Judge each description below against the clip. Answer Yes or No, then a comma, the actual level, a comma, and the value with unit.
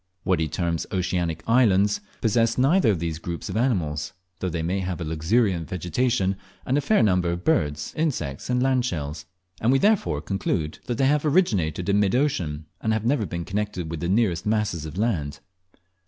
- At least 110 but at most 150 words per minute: No, average, 185 wpm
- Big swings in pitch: Yes, wide, 6.4 semitones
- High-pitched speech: No, very low, 95 Hz